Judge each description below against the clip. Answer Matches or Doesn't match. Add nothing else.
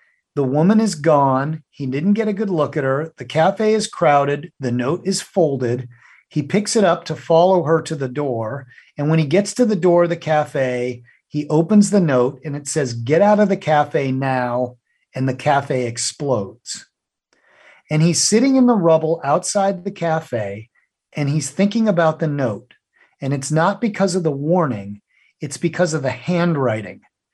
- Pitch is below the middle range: Doesn't match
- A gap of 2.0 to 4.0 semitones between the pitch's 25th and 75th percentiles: Doesn't match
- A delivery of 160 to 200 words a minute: Matches